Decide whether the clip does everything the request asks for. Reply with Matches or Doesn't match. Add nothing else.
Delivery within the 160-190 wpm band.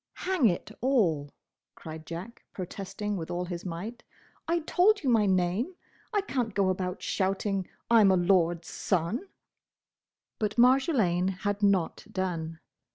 Doesn't match